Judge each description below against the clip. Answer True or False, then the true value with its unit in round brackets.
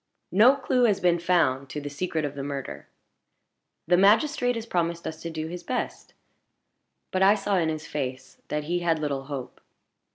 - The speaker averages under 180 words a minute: False (185 wpm)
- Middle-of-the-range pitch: True (170 Hz)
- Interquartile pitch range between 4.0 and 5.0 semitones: True (4.7 semitones)